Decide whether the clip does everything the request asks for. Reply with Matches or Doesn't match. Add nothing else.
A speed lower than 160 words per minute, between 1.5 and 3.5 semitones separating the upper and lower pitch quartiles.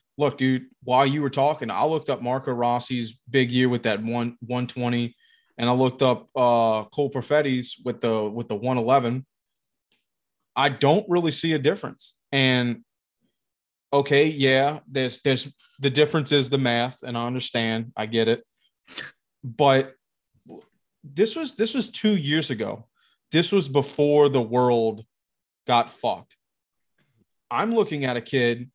Matches